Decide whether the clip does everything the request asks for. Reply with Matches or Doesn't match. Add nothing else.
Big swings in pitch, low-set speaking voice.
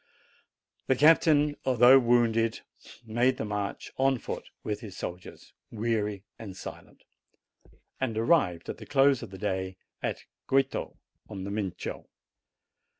Doesn't match